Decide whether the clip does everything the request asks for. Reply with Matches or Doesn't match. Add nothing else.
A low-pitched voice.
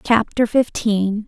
Doesn't match